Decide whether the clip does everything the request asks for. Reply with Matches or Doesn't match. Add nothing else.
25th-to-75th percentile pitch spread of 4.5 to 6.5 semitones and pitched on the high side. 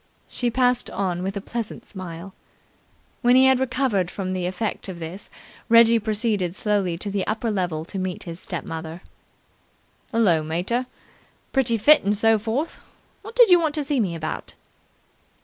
Matches